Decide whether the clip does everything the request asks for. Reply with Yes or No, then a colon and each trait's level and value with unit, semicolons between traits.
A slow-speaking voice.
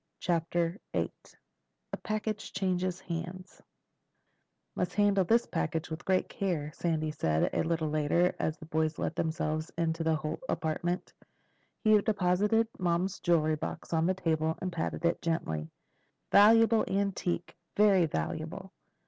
Yes: slow, 130 wpm